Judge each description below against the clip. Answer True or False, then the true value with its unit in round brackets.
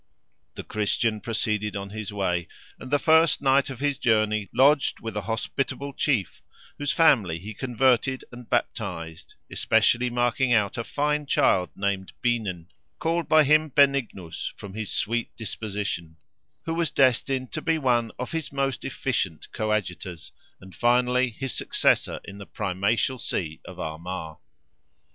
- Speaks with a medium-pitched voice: False (115 Hz)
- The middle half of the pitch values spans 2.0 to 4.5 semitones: False (5.2 semitones)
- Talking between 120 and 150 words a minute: True (145 wpm)